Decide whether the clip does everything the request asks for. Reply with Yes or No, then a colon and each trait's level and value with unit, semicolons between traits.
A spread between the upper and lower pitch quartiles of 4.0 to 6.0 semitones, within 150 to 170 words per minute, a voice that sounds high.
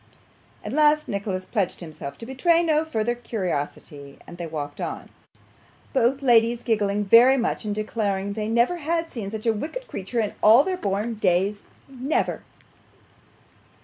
Yes: average, 5.0 semitones; average, 155 wpm; high, 225 Hz